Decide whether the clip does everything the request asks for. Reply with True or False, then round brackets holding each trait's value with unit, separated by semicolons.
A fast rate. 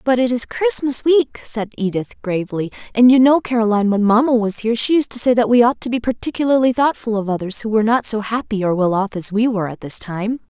True (245 wpm)